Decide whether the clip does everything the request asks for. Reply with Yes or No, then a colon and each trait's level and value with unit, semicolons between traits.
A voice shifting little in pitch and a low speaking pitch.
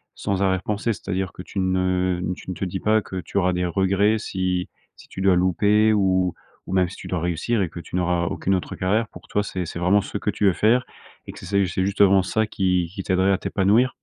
Yes: narrow, 1.9 semitones; very low, 95 Hz